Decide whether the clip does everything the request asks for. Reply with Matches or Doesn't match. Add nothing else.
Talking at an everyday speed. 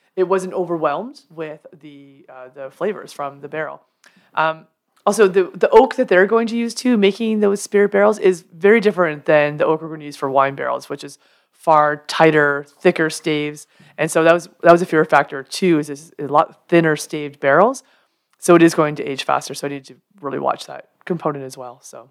Doesn't match